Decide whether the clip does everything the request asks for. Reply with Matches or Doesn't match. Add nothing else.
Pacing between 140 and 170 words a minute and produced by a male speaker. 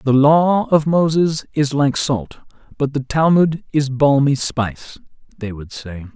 Matches